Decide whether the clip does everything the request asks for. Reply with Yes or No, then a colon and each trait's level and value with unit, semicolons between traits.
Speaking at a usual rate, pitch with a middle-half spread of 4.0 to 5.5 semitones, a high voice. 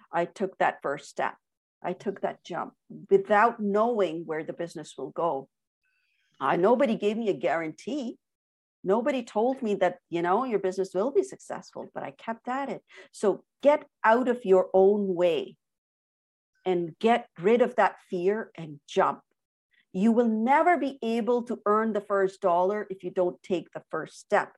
Yes: average, 170 wpm; average, 4.6 semitones; high, 200 Hz